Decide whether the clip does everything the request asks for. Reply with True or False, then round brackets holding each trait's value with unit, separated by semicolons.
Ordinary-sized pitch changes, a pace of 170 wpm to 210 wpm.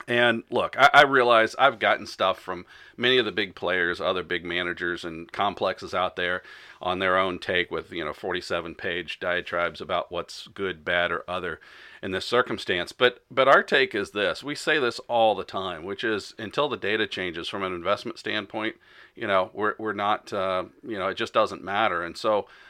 True (3.0 semitones; 200 wpm)